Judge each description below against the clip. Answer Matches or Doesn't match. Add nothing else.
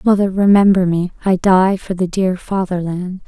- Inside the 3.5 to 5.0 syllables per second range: Matches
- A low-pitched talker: Doesn't match